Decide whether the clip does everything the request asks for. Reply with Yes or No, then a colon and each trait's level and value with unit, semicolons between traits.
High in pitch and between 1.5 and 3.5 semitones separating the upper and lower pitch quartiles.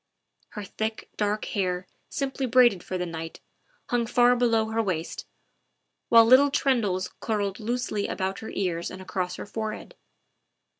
No: high, 215 Hz; average, 4.3 semitones